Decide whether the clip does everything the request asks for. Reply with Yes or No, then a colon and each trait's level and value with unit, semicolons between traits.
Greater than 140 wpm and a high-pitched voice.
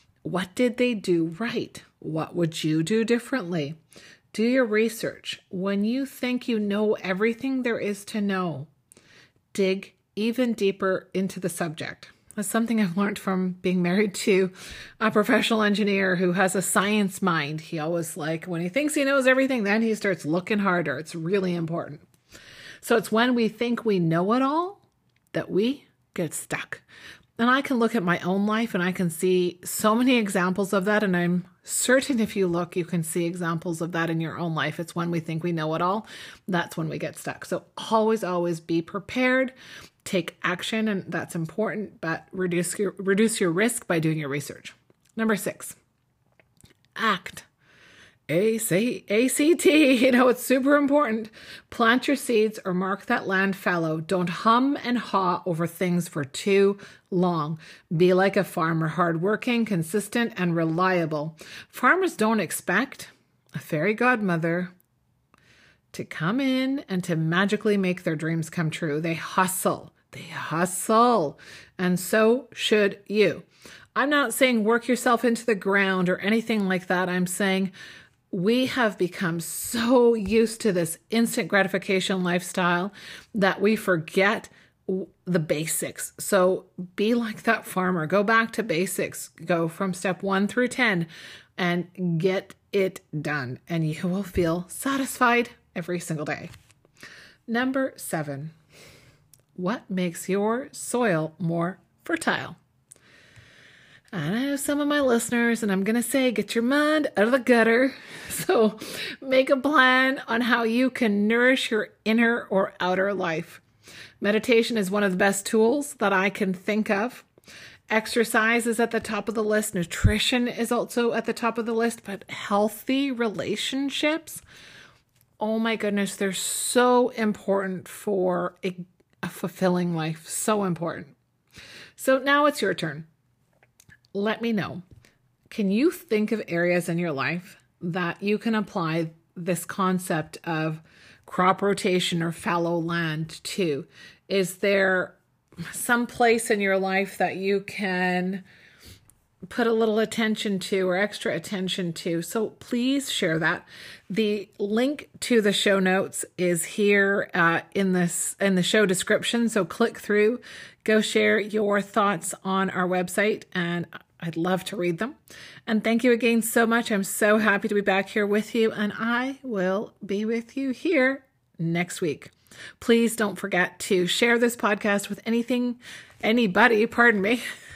Yes: average, 155 wpm; high, 200 Hz